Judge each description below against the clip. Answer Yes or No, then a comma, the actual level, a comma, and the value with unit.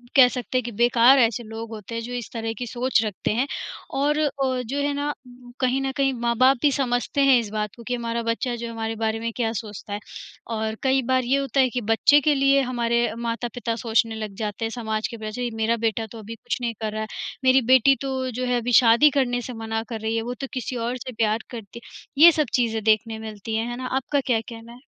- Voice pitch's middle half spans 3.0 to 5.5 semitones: No, narrow, 2.6 semitones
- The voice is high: Yes, high, 235 Hz